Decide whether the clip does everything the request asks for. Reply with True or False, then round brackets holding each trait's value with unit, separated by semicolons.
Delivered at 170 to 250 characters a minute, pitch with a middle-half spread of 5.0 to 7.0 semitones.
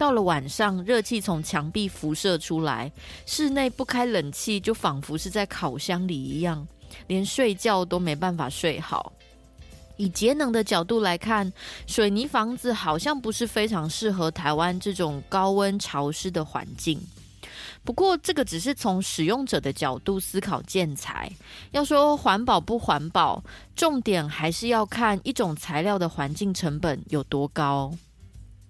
True (230 characters per minute; 6.0 semitones)